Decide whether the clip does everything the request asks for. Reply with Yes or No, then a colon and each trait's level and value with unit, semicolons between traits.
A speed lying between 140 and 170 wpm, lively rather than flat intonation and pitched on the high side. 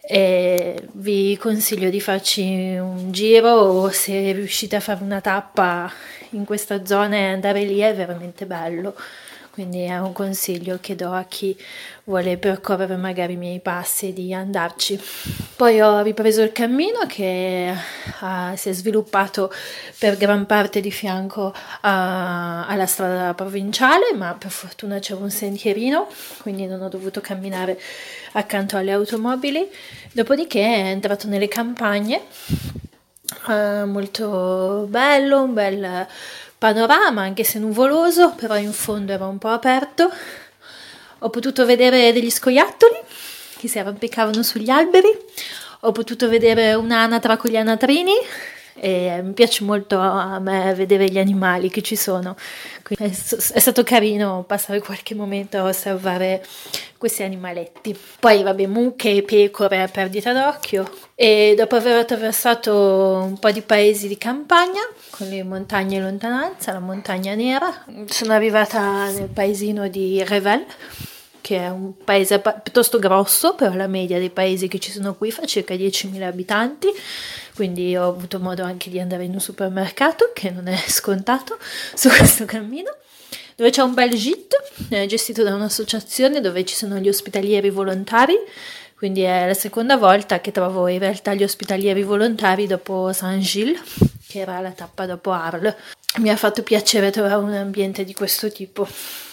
No: average, 150 wpm; average, 3.0 semitones; high, 205 Hz